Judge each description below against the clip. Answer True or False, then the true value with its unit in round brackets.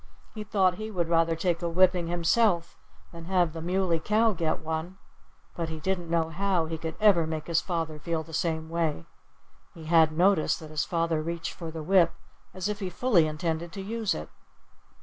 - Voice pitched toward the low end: False (170 Hz)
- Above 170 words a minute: True (195 wpm)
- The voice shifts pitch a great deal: False (2.5 semitones)